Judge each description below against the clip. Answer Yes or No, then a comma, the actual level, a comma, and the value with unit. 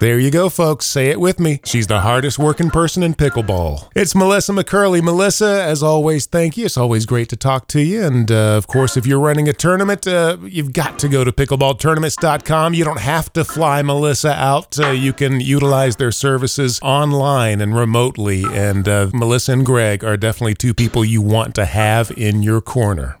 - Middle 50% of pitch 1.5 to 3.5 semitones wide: No, average, 5.3 semitones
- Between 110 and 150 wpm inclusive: No, average, 200 wpm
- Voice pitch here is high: No, low, 135 Hz